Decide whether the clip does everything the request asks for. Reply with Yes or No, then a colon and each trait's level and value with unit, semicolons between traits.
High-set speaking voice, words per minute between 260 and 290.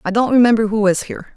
Yes: high, 220 Hz; fast, 265 wpm